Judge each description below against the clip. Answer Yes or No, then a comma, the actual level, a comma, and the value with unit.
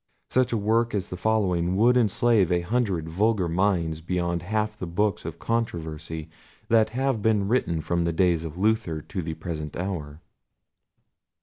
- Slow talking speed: No, average, 165 wpm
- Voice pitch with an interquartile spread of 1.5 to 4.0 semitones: No, average, 4.6 semitones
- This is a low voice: Yes, very low, 95 Hz